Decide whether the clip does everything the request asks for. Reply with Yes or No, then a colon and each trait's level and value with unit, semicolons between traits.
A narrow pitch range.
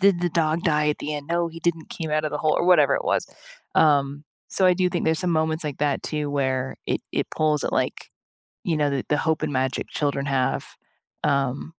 Yes: narrow, 2.3 semitones